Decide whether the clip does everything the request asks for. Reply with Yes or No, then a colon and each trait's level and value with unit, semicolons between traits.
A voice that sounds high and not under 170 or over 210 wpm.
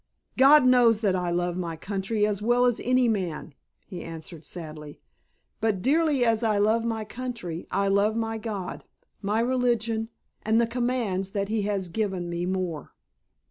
No: high, 210 Hz; average, 160 wpm